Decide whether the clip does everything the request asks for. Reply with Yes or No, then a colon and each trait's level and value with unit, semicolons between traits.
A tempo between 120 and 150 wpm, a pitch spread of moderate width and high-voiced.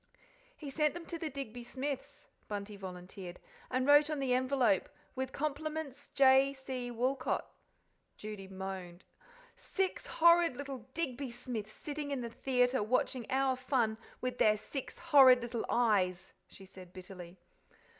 Yes: average, 140 wpm; average, 4.6 semitones; very high, 255 Hz